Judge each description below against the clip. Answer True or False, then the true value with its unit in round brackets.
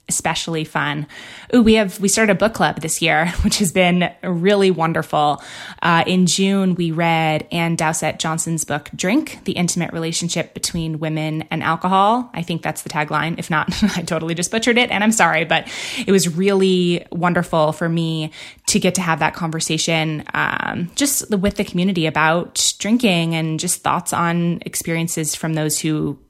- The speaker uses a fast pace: False (175 wpm)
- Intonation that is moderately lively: True (3.1 semitones)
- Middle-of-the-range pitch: True (170 Hz)